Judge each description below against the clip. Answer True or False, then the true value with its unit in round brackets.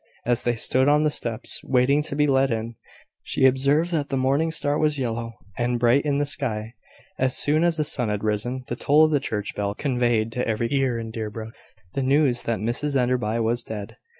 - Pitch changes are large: False (3.8 semitones)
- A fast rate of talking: True (210 wpm)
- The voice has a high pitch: False (125 Hz)